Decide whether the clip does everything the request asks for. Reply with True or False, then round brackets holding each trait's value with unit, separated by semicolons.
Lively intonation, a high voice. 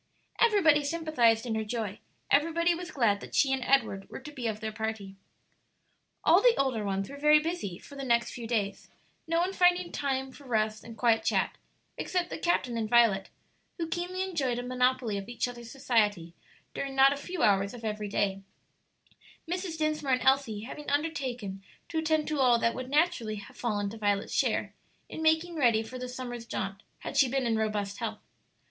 True (5.7 semitones; 250 Hz)